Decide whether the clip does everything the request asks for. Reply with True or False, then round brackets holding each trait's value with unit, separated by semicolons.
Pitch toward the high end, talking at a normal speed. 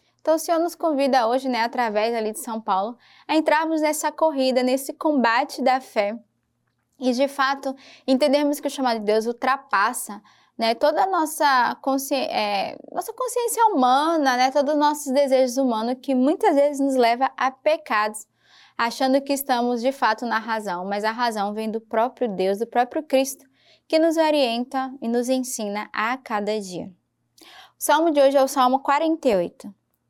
True (260 Hz; 170 wpm)